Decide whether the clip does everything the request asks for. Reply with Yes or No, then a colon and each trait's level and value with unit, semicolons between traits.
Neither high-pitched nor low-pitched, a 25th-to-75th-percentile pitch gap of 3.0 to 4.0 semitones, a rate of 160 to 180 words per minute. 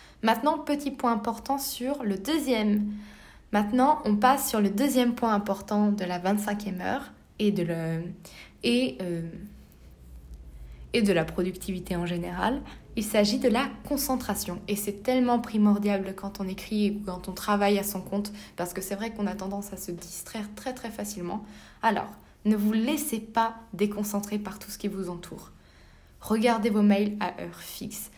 No: high, 205 Hz; average, 3.7 semitones; average, 170 wpm